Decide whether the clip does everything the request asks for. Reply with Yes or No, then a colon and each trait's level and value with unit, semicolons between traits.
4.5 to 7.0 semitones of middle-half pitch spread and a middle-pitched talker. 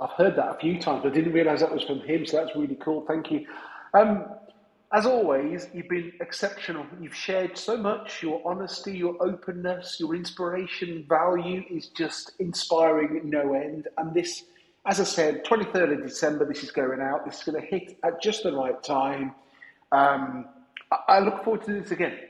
No: average, 3.8 semitones; medium, 175 Hz